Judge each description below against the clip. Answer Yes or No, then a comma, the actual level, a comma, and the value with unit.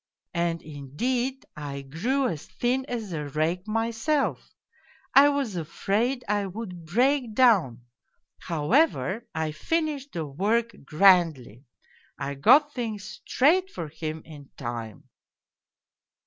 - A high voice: Yes, high, 195 Hz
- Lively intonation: Yes, wide, 8.4 semitones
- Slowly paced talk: Yes, slow, 115 wpm